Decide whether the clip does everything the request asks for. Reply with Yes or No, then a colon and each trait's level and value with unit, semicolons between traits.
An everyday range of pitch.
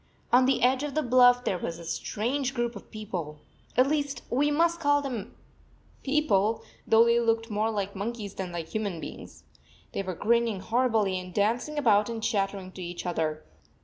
Yes: average, 4.6 semitones